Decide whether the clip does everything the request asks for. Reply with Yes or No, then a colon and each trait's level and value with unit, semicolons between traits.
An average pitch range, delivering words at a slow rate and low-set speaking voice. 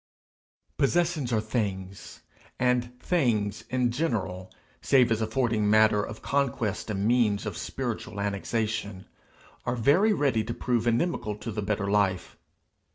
Yes: average, 3.3 semitones; slow, 130 wpm; low, 110 Hz